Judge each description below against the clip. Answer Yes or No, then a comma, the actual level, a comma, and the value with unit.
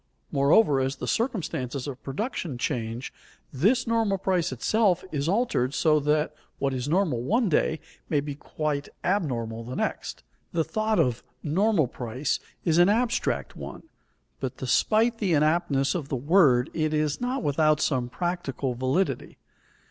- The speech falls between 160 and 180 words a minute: No, average, 150 wpm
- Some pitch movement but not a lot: No, wide, 6.3 semitones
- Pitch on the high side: No, medium, 155 Hz